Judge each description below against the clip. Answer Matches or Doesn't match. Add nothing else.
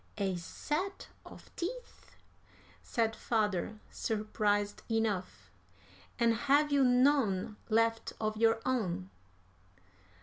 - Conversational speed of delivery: Doesn't match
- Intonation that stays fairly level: Doesn't match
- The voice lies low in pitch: Doesn't match